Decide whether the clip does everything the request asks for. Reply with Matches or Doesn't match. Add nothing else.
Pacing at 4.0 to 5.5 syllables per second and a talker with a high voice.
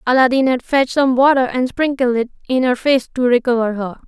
Doesn't match